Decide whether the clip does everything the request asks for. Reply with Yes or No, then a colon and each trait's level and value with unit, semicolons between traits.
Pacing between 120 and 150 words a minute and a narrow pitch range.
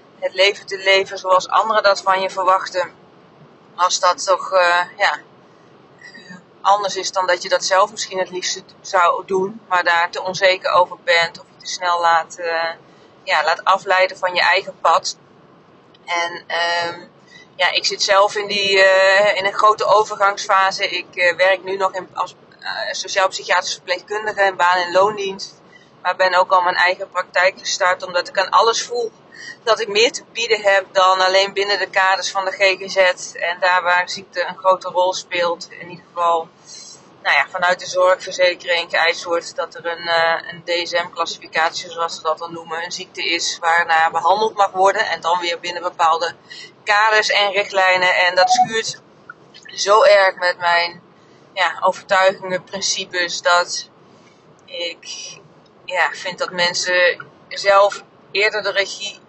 No: average, 165 wpm; narrow, 1.9 semitones